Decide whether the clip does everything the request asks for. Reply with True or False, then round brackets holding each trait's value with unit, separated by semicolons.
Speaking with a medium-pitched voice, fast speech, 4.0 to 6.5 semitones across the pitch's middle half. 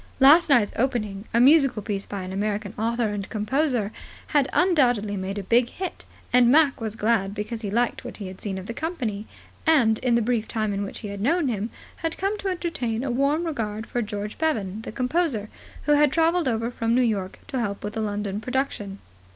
False (230 Hz; 210 wpm; 4.9 semitones)